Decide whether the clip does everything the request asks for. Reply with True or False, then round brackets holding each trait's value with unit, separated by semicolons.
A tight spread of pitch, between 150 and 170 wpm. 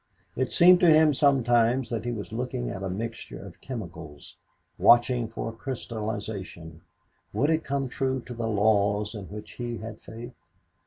False (3.7 semitones; 165 wpm)